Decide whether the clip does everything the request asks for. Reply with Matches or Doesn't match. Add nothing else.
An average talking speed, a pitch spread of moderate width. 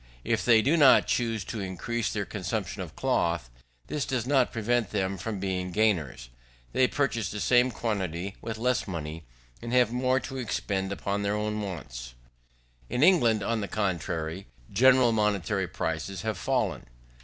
Matches